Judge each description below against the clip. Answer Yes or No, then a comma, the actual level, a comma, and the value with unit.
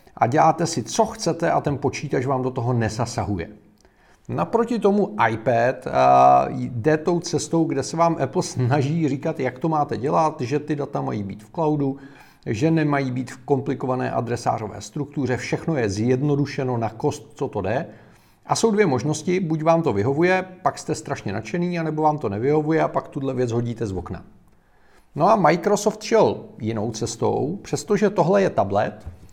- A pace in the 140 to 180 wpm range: Yes, fast, 170 wpm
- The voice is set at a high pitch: No, medium, 140 Hz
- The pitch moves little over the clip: No, average, 5.3 semitones